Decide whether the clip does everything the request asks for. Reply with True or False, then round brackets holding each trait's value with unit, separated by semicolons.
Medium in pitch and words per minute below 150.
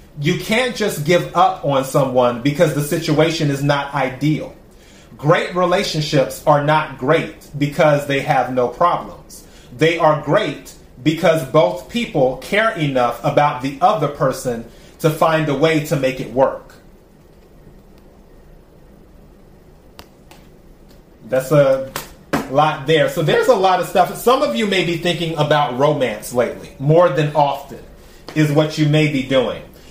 True (155 Hz; 140 wpm)